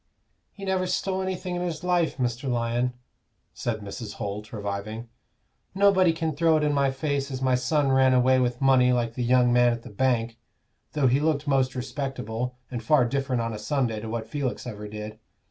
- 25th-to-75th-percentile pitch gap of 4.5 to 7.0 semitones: No, average, 3.9 semitones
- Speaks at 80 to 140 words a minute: No, average, 195 wpm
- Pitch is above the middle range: No, low, 130 Hz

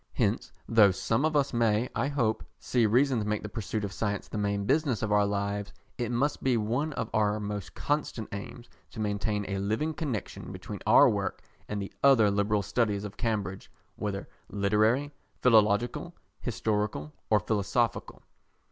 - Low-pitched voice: Yes, low, 110 Hz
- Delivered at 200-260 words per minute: No, average, 165 wpm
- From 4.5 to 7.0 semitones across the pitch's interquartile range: No, average, 3.0 semitones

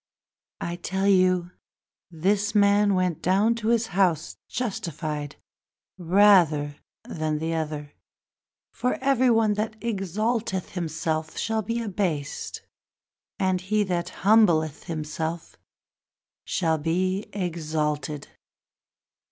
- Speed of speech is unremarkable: No, slow, 100 wpm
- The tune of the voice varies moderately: Yes, average, 4.7 semitones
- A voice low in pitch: No, medium, 185 Hz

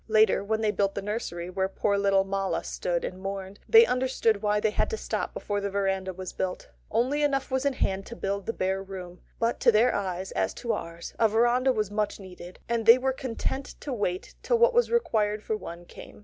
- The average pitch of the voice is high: Yes, high, 210 Hz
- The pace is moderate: No, fast, 220 wpm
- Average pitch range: Yes, average, 3.8 semitones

